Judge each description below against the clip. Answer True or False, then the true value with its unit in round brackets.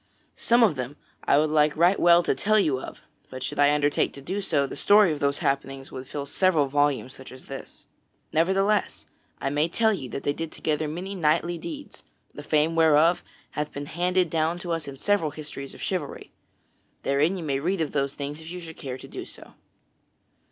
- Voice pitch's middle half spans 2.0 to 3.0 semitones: False (3.7 semitones)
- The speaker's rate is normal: False (210 wpm)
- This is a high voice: False (155 Hz)